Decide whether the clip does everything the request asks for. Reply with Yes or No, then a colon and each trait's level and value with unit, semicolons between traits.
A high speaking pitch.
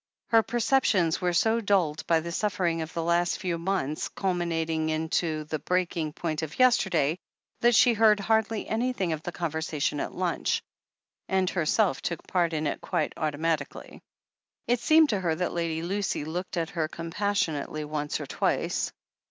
No: medium, 170 Hz